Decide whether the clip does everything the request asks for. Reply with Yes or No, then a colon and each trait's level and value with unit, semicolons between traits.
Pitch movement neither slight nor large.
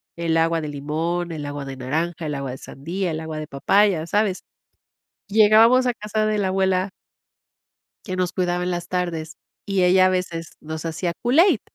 Yes: average, 3.5 semitones